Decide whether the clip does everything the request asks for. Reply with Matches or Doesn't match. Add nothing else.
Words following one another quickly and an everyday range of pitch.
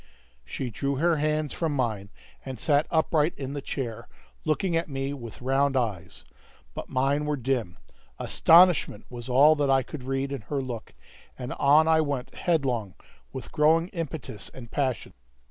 Doesn't match